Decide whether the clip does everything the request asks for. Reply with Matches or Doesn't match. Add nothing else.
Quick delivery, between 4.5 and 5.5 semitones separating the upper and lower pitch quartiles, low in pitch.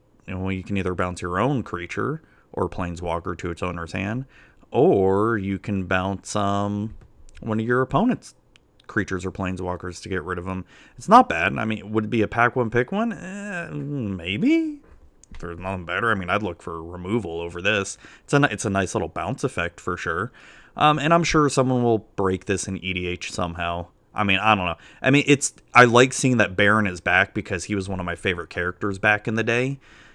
Matches